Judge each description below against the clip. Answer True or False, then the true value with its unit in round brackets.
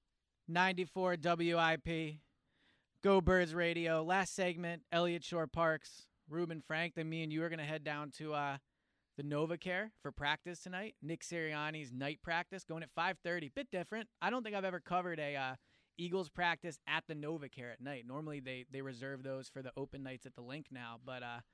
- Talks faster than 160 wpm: True (190 wpm)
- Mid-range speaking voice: True (160 Hz)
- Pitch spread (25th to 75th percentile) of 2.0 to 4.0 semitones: True (3.5 semitones)